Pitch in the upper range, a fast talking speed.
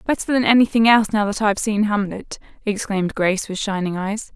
No: high, 210 Hz; average, 195 wpm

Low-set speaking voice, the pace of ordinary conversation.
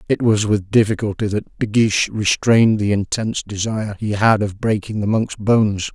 Yes: low, 105 Hz; average, 180 wpm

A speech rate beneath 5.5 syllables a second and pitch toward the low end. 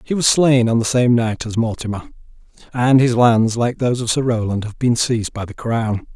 Yes: 5.2 syllables/s; low, 120 Hz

